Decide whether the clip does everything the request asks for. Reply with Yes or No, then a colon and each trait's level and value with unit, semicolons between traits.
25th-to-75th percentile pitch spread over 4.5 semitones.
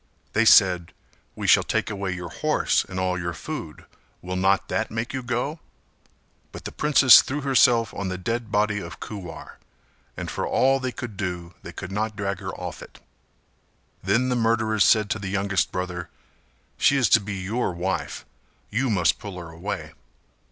No: average, 3.9 semitones